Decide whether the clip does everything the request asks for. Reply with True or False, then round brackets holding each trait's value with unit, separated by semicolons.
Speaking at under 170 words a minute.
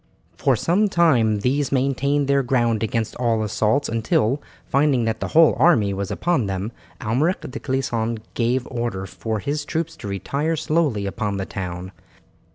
True (160 wpm)